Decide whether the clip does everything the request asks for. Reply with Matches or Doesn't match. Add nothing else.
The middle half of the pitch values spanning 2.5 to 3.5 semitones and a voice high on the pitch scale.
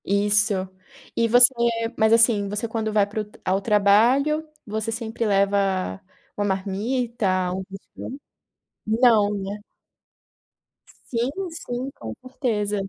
Matches